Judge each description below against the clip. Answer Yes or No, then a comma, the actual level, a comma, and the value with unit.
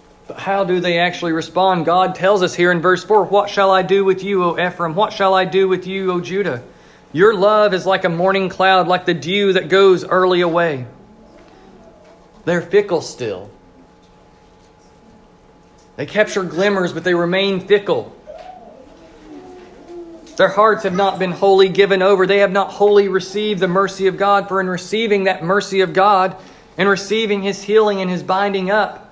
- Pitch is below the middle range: No, high, 190 Hz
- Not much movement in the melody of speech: Yes, narrow, 1.9 semitones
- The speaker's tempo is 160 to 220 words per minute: Yes, average, 175 wpm